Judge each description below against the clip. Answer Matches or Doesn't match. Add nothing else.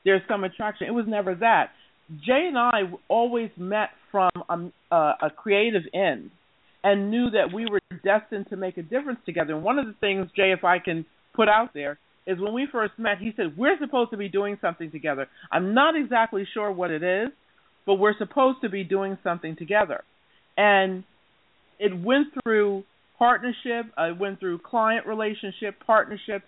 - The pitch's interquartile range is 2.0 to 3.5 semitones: Matches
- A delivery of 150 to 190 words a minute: Matches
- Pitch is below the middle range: Doesn't match